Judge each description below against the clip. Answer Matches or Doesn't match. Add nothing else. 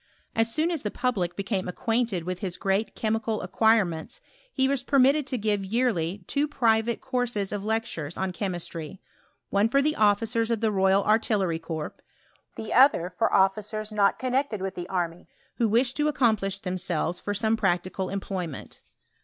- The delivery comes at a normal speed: Matches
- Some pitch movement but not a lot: Matches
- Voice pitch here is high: Matches